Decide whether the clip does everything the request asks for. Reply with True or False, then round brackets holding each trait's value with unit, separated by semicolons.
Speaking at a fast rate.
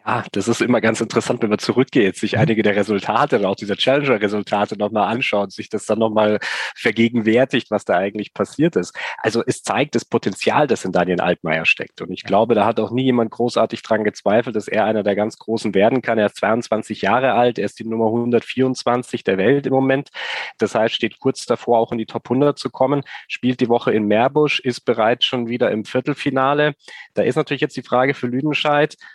True (210 wpm)